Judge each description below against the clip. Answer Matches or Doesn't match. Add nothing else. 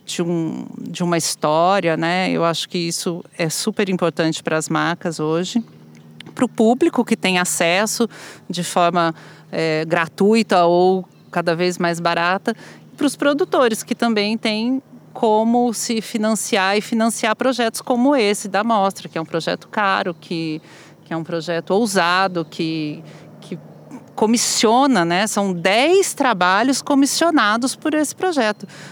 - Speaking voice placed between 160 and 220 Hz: Matches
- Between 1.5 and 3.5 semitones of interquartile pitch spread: Doesn't match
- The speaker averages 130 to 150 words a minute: Matches